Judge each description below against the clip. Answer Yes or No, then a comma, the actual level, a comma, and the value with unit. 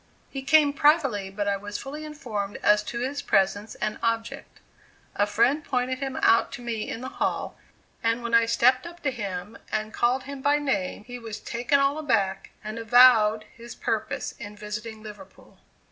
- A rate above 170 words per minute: Yes, average, 180 wpm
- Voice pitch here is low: No, high, 235 Hz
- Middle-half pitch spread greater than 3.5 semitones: Yes, average, 4.2 semitones